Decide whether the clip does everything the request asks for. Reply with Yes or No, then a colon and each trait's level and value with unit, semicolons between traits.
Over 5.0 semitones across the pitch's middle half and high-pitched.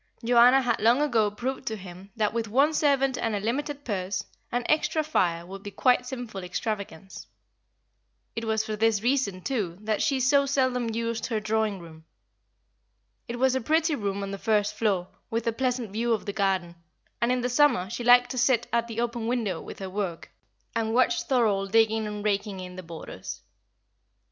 No: average, 3.7 semitones; high, 225 Hz